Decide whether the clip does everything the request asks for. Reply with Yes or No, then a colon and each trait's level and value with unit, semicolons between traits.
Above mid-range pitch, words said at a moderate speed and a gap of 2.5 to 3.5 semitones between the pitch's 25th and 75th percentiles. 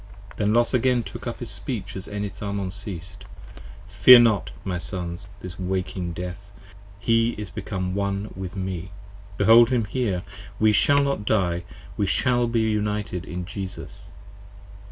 No: low, 100 Hz; average, 145 wpm; average, 3.1 semitones